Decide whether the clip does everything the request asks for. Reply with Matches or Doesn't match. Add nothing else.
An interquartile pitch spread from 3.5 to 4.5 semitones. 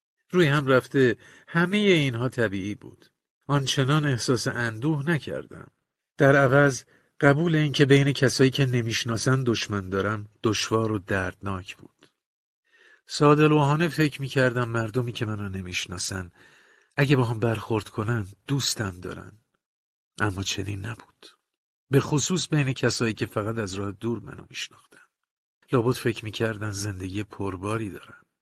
Doesn't match